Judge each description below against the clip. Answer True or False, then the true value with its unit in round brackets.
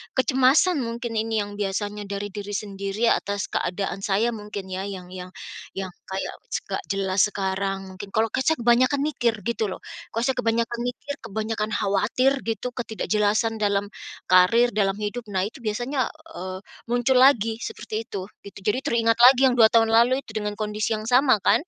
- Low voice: False (220 Hz)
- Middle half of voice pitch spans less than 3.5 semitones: True (3.1 semitones)